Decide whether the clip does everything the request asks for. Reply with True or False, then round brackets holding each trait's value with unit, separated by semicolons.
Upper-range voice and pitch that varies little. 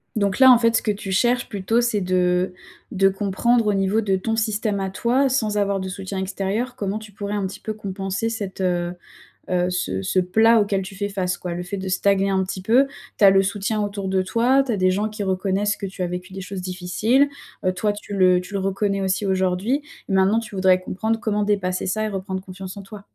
True (195 Hz; 2.3 semitones)